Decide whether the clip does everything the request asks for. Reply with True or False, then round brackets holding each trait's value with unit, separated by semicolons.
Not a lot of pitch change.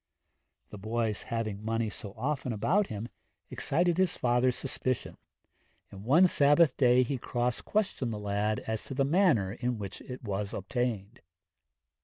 False (4.4 semitones)